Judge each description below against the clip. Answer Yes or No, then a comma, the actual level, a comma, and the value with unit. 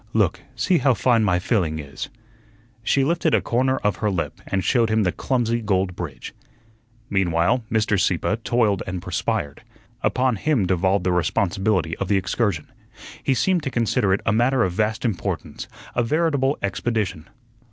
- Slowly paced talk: No, average, 165 wpm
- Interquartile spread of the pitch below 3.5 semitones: No, average, 4.7 semitones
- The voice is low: Yes, low, 105 Hz